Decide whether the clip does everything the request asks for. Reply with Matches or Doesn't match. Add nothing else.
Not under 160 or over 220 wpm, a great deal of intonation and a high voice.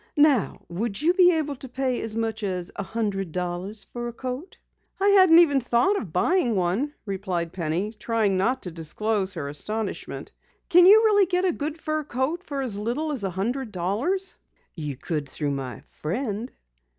Matches